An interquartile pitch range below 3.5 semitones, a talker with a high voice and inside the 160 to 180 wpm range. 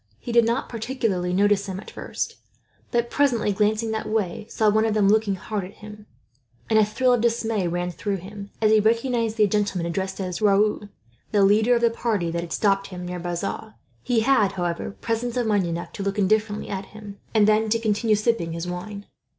No: narrow, 2.5 semitones; high, 210 Hz; fast, 205 wpm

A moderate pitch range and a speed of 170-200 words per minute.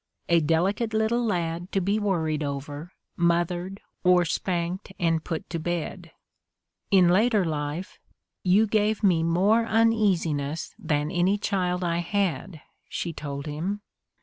No: average, 3.6 semitones; slow, 135 wpm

